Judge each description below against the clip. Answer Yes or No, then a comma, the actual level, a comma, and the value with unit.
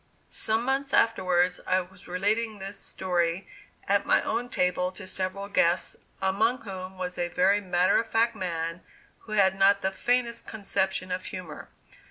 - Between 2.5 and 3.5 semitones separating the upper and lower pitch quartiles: Yes, average, 2.8 semitones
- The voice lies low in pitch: No, high, 190 Hz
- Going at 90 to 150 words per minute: No, average, 160 wpm